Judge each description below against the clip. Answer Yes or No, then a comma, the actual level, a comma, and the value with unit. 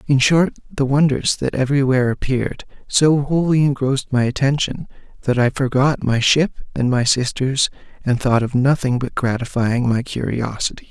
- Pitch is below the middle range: Yes, low, 130 Hz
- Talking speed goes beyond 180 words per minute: No, average, 155 wpm